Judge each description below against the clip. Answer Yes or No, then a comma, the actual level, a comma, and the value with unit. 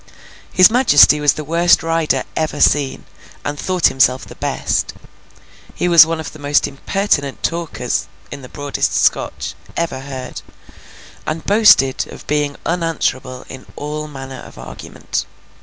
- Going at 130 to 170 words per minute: Yes, average, 140 wpm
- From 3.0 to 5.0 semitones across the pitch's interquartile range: Yes, average, 3.5 semitones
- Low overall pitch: No, medium, 150 Hz